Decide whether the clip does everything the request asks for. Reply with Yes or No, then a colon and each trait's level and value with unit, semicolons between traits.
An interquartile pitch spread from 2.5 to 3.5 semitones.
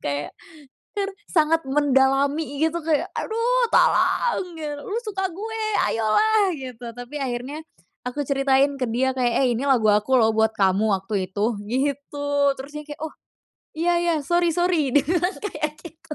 No: wide, 5.5 semitones